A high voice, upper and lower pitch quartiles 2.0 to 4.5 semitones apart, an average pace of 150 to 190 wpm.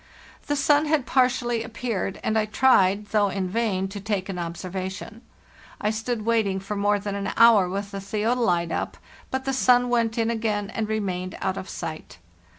Yes: high, 210 Hz; average, 3.1 semitones; average, 180 wpm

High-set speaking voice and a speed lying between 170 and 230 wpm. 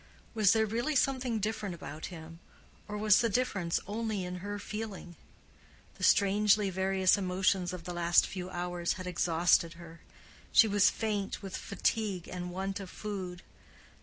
No: high, 195 Hz; average, 155 wpm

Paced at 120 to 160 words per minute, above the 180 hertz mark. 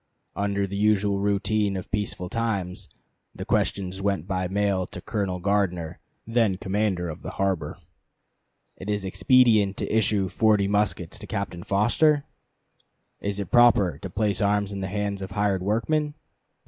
No: average, 150 wpm; low, 100 Hz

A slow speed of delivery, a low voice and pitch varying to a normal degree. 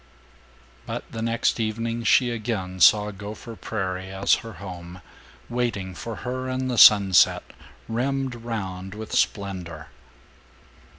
Yes: slow, 120 wpm; low, 110 Hz; average, 3.7 semitones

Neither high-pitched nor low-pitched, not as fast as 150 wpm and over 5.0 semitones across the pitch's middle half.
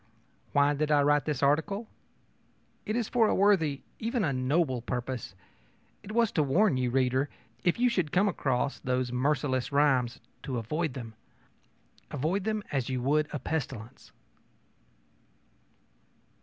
Yes: medium, 145 Hz; average, 140 wpm; wide, 5.4 semitones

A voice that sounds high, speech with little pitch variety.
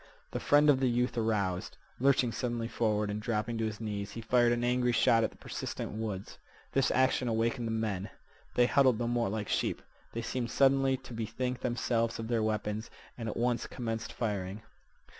No: low, 115 Hz; narrow, 2.2 semitones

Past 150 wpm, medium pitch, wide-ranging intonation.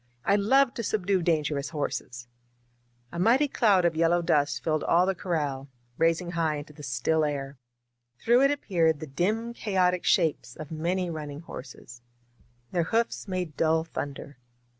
No: average, 160 wpm; medium, 165 Hz; average, 4.3 semitones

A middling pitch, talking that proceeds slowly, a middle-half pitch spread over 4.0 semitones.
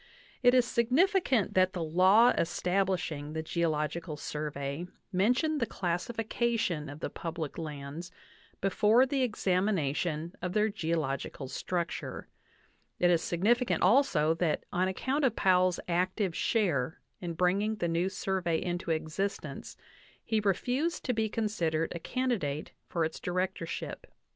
Yes: medium, 180 Hz; slow, 130 wpm; average, 5.0 semitones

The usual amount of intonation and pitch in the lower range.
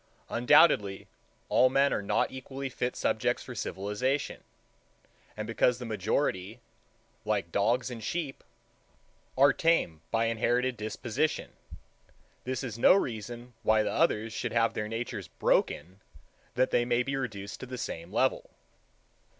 Yes: average, 3.4 semitones; low, 120 Hz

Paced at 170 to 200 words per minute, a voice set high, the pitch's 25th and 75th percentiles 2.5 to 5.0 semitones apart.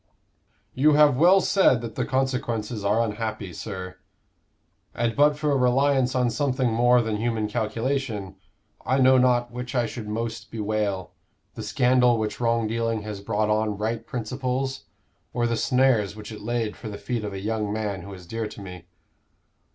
No: average, 175 wpm; low, 115 Hz; average, 3.0 semitones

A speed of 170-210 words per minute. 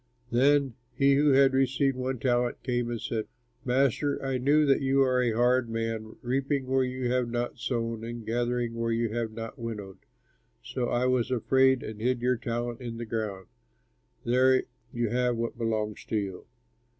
Yes: average, 175 wpm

